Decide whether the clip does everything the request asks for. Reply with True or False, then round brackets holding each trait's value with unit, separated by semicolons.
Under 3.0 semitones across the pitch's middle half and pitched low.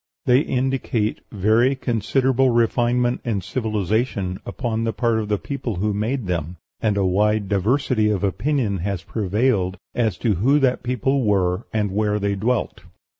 False (3.8 semitones; 110 Hz)